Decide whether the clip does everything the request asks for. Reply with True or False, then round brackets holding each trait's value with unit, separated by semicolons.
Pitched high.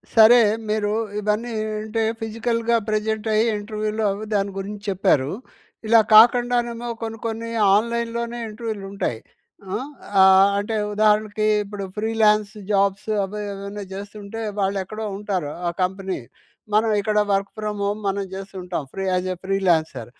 True (210 Hz)